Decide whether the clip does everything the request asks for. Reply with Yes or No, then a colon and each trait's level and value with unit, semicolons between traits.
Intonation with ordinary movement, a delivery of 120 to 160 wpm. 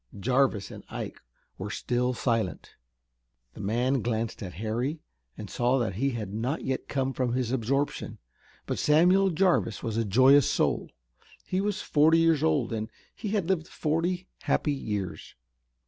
No: wide, 5.8 semitones; average, 155 wpm